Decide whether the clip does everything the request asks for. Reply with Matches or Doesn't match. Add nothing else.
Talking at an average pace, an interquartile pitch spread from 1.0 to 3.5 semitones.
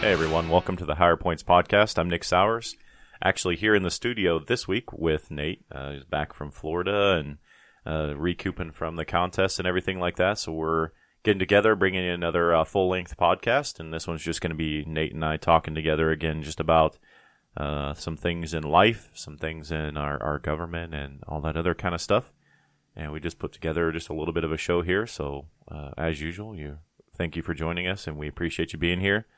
Doesn't match